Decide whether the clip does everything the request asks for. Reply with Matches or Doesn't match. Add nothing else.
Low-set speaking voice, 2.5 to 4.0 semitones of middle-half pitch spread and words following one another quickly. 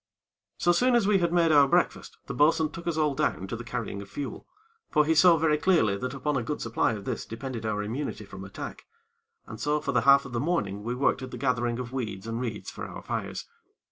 Doesn't match